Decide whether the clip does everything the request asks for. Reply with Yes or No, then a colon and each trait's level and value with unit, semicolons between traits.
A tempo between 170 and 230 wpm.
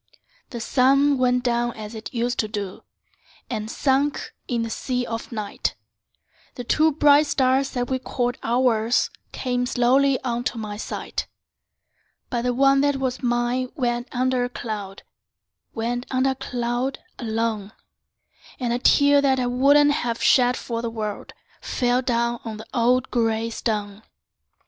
No: average, 150 wpm